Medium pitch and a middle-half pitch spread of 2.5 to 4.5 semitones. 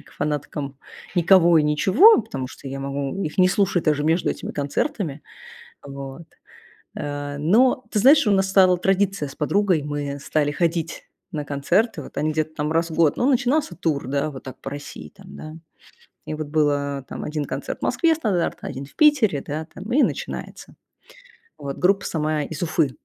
No: medium, 155 Hz; average, 5.0 semitones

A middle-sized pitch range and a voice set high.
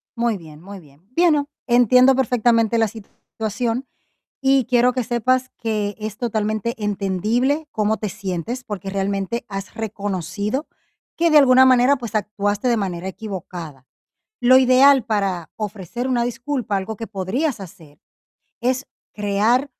Yes: average, 4.1 semitones; high, 220 Hz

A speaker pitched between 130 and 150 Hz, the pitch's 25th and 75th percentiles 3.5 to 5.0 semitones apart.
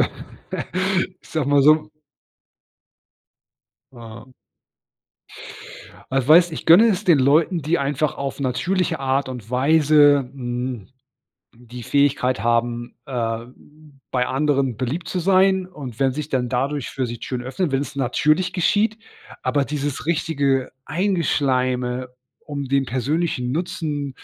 Yes: medium, 140 Hz; average, 3.8 semitones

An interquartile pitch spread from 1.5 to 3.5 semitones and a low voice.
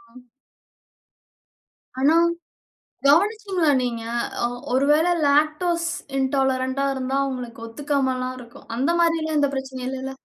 No: average, 3.2 semitones; very high, 270 Hz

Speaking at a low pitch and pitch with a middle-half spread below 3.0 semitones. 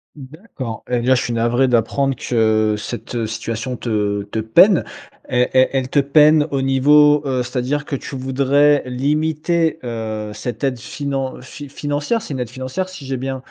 No: low, 130 Hz; average, 3.5 semitones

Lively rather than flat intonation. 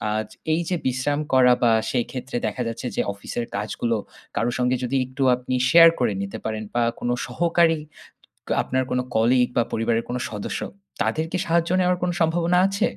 Yes: wide, 5.9 semitones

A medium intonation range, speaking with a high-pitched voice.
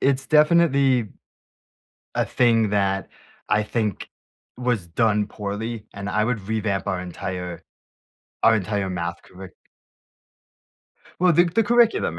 No: average, 4.9 semitones; low, 110 Hz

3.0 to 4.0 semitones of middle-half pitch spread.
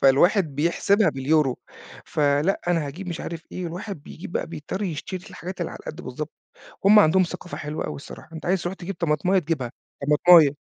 Yes: average, 3.6 semitones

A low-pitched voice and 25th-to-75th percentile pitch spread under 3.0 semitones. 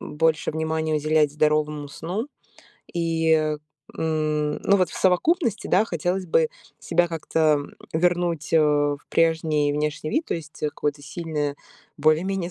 No: medium, 160 Hz; narrow, 2.6 semitones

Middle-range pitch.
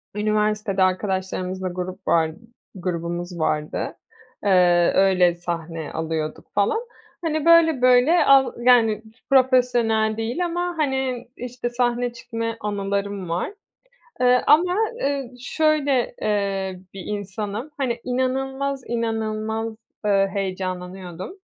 No: high, 215 Hz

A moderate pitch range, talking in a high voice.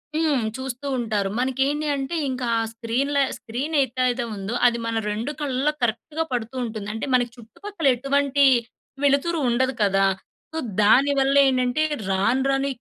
Yes: average, 3.1 semitones; very high, 260 Hz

